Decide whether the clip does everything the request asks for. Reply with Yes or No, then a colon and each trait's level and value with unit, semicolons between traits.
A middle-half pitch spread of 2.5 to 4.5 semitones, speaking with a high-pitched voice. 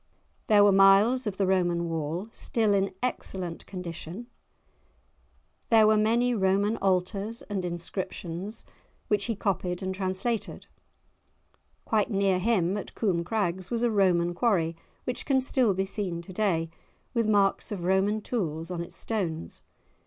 Yes: average, 3.4 semitones; high, 195 Hz